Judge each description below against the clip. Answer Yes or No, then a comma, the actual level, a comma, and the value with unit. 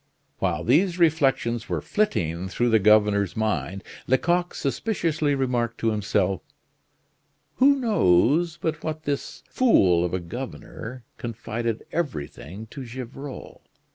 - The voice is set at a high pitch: No, low, 120 Hz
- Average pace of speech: No, slow, 115 wpm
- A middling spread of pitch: No, wide, 7.0 semitones